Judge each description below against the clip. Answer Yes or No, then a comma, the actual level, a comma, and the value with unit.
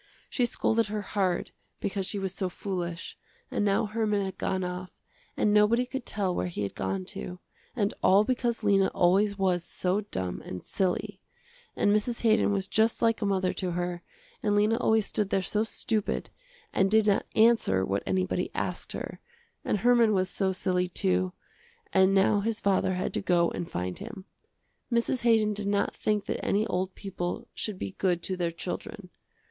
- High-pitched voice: Yes, high, 195 Hz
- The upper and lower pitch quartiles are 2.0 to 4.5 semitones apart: Yes, average, 2.8 semitones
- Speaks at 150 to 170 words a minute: No, average, 185 wpm